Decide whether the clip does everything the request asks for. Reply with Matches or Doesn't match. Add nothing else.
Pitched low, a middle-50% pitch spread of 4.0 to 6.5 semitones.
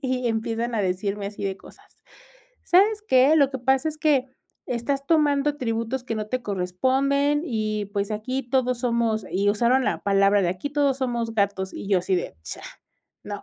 Doesn't match